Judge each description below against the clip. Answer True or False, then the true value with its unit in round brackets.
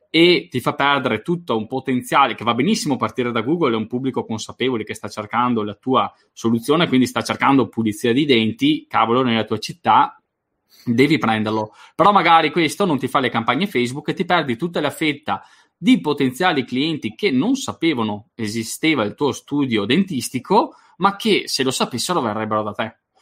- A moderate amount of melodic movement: False (5.8 semitones)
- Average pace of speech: False (180 wpm)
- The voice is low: True (125 Hz)